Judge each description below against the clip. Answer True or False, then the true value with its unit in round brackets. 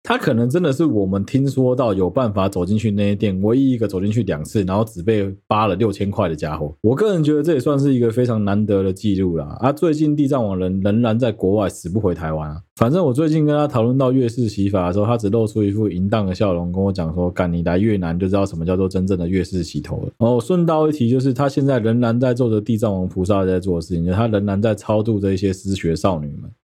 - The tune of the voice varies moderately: True (4.4 semitones)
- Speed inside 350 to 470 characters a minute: True (385 characters per minute)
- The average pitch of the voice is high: False (105 Hz)